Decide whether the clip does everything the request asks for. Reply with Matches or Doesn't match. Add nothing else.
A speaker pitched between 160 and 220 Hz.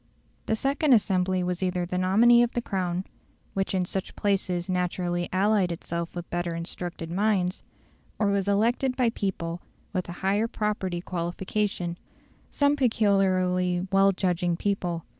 Matches